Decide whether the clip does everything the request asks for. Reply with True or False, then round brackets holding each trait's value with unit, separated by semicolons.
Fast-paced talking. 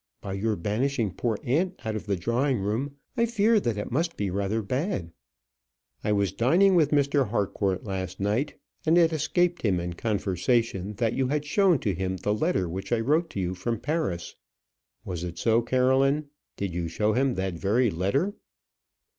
False (180 wpm)